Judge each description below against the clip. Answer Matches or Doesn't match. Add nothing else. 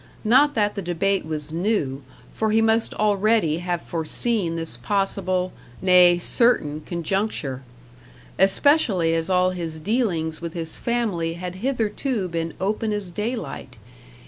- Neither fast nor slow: Doesn't match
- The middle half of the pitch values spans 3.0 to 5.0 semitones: Matches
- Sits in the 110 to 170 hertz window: Doesn't match